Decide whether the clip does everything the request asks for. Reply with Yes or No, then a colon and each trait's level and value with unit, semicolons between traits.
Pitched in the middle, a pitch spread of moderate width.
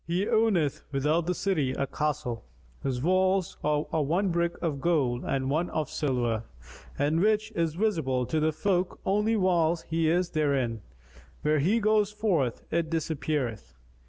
Yes: medium, 160 Hz; average, 4.8 semitones